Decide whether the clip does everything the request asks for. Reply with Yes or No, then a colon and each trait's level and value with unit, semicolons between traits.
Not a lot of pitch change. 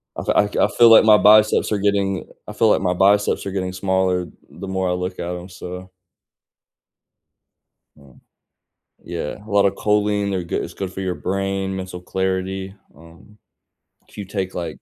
Yes: narrow, 1.9 semitones